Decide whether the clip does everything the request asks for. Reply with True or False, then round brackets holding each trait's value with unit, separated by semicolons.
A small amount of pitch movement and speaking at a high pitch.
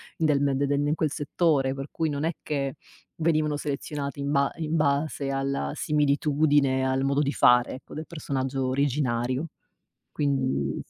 False (1.7 semitones; 140 Hz)